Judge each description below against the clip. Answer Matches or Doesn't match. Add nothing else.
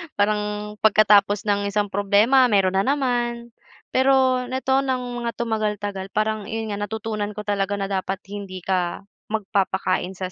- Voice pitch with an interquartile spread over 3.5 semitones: Doesn't match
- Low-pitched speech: Doesn't match